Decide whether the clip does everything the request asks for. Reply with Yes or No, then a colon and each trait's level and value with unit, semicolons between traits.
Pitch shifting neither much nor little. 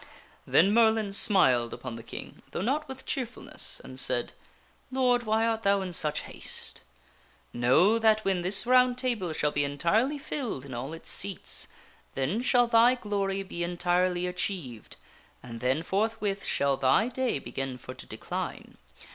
No: wide, 7.6 semitones